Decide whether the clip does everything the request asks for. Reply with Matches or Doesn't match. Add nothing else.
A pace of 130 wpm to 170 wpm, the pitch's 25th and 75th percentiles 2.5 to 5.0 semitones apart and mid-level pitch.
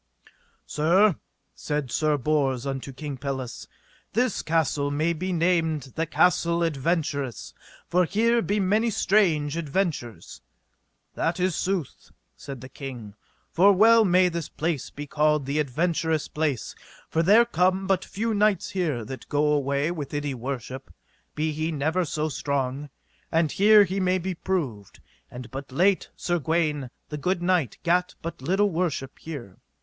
Matches